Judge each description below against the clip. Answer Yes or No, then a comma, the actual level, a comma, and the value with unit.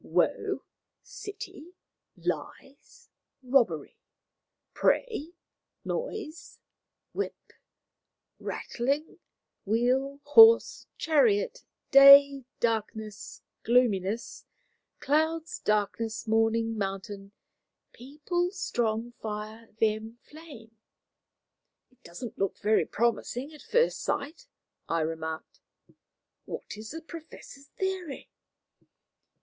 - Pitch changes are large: Yes, wide, 6.4 semitones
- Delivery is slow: Yes, slow, 80 wpm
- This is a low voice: No, very high, 250 Hz